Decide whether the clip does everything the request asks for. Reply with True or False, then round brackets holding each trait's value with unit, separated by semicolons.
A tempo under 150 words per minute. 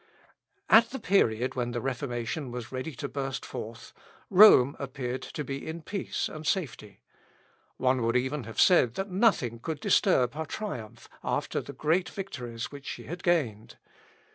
False (160 wpm)